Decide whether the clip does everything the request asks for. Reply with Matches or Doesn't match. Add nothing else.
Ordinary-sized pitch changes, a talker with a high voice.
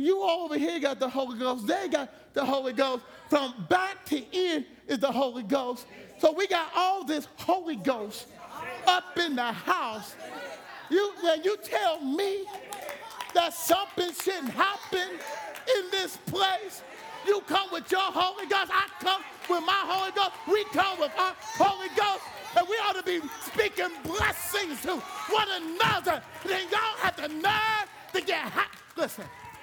Matches